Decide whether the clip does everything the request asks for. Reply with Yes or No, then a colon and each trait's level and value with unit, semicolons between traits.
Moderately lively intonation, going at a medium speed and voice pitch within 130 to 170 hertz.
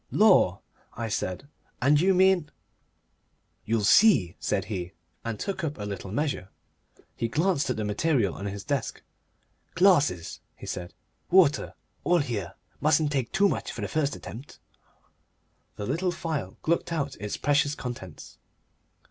No: wide, 8.0 semitones; average, 150 wpm; medium, 140 Hz